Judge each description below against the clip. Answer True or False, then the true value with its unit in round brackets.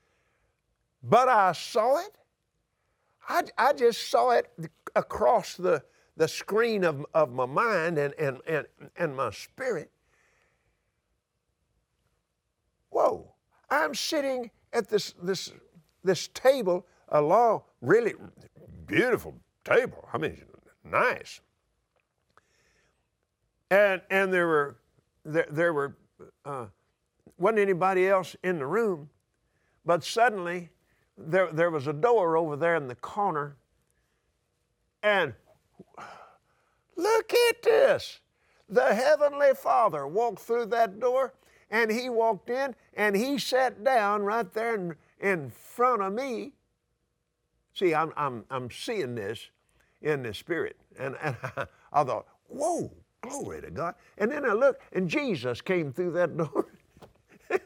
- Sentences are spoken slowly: True (125 wpm)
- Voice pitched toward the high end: True (195 Hz)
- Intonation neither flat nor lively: False (7.3 semitones)